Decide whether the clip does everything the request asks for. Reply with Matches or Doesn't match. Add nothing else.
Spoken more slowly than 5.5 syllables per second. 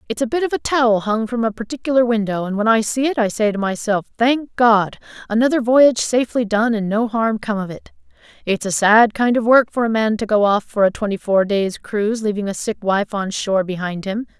Doesn't match